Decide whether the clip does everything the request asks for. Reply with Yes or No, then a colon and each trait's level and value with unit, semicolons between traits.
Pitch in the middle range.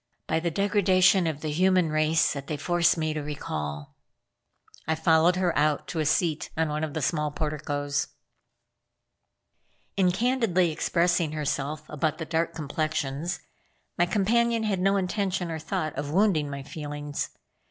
Yes: medium, 160 Hz